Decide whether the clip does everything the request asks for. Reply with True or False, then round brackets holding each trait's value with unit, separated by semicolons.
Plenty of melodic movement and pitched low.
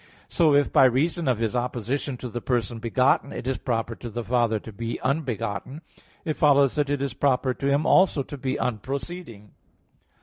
False (3.3 semitones; 130 Hz)